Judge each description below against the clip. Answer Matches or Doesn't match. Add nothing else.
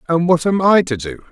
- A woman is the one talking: Doesn't match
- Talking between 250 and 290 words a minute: Matches